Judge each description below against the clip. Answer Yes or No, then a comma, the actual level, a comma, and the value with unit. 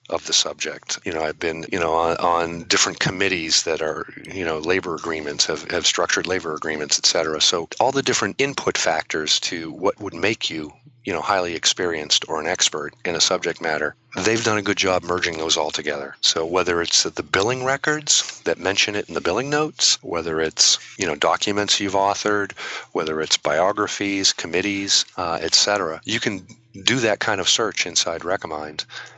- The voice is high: No, low, 100 Hz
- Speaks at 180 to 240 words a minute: Yes, average, 190 wpm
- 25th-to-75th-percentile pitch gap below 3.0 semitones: No, average, 4.5 semitones